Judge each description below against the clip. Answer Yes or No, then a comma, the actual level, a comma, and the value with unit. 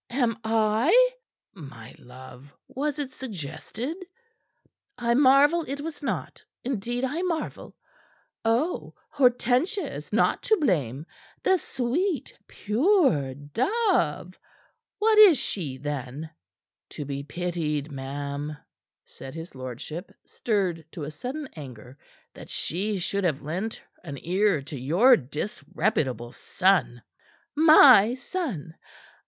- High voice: Yes, high, 195 Hz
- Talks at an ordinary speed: No, slow, 110 wpm